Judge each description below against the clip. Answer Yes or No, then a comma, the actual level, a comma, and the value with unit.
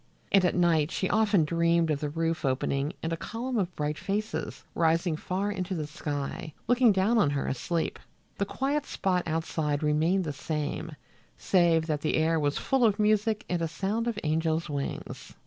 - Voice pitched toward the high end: No, medium, 170 Hz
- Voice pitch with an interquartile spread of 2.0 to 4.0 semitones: No, average, 4.5 semitones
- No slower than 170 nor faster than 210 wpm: Yes, average, 180 wpm